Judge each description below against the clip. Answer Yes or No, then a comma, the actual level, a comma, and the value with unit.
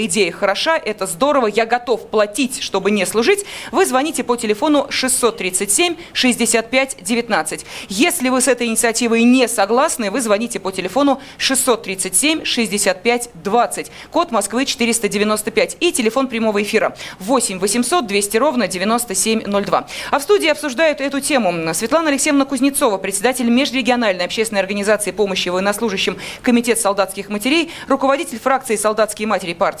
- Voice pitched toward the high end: Yes, high, 235 Hz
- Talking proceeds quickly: No, average, 130 wpm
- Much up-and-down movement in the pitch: No, average, 4.7 semitones